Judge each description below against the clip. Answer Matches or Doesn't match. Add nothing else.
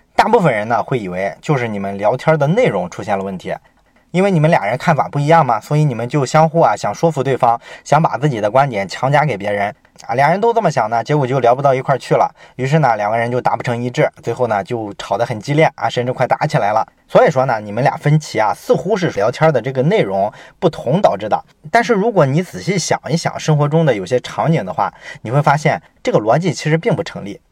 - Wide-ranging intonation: Matches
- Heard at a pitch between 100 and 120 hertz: Doesn't match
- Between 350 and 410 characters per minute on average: Matches